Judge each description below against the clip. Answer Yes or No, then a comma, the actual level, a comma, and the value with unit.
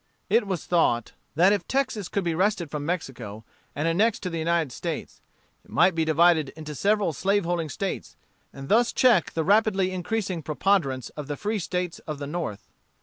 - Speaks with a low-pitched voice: No, medium, 175 Hz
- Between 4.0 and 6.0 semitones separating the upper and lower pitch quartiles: Yes, average, 4.5 semitones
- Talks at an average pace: Yes, average, 180 wpm